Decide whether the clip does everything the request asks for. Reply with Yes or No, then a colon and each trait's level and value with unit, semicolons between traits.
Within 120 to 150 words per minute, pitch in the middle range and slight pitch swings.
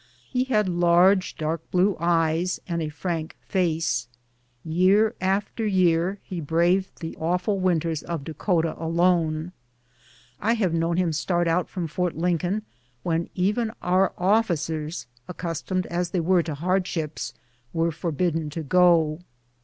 Yes: slow, 135 wpm; medium, 175 Hz; narrow, 2.2 semitones